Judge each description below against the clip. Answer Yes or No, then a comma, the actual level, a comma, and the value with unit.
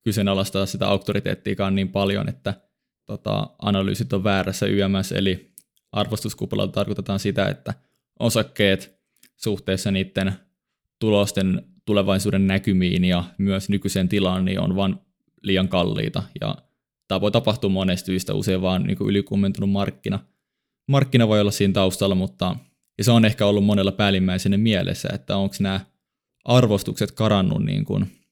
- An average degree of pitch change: No, narrow, 1.1 semitones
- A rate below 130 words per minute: No, average, 135 wpm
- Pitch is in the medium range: No, low, 100 Hz